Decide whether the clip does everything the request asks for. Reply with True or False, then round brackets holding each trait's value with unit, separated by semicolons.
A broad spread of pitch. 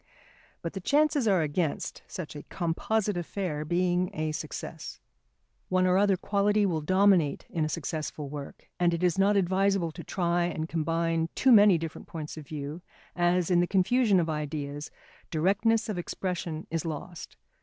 False (3.6 semitones)